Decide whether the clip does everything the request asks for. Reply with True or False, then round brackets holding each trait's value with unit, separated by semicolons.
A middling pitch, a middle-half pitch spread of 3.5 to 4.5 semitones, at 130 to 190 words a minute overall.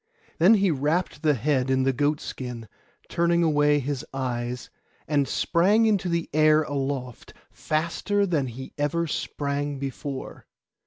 True (145 Hz; 4.0 semitones; 140 wpm)